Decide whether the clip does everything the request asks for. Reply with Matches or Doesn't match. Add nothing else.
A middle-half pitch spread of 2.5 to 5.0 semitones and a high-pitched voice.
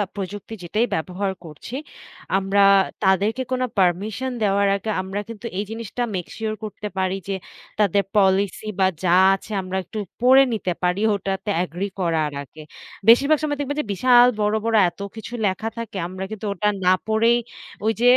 Matches